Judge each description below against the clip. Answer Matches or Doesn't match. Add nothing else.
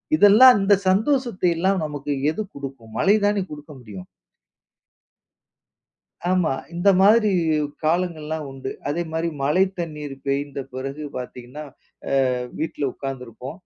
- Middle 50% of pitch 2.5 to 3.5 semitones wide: Doesn't match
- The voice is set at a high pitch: Doesn't match